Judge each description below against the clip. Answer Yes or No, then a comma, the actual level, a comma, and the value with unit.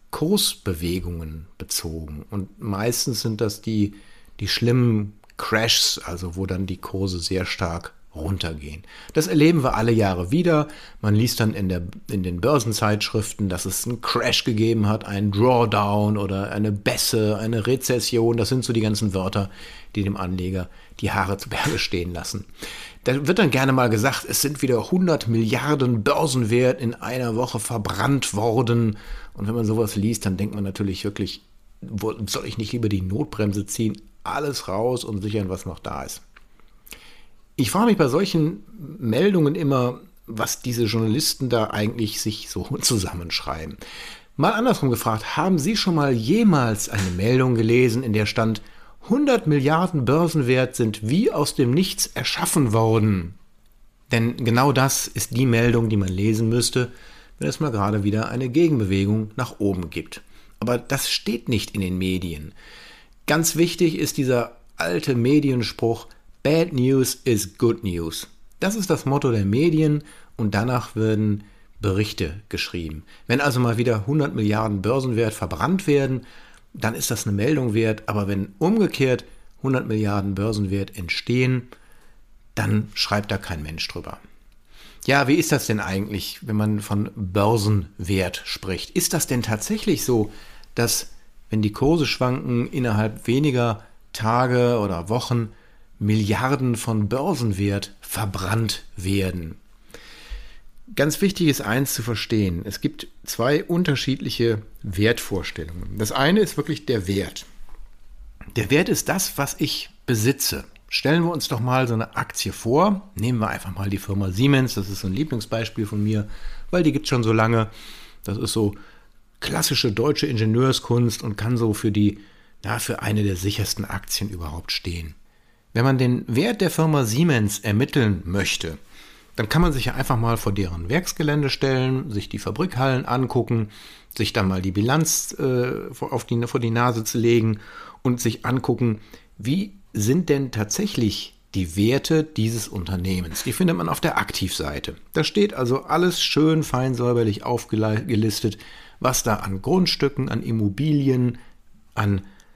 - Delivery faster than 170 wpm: No, average, 155 wpm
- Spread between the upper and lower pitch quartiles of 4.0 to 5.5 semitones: Yes, average, 4.4 semitones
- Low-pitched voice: Yes, low, 115 Hz